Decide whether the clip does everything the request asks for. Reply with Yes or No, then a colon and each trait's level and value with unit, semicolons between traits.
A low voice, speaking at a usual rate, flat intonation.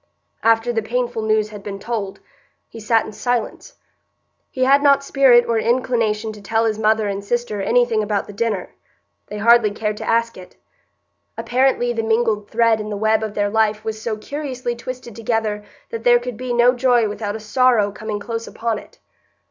No: high, 225 Hz; average, 190 wpm; narrow, 2.2 semitones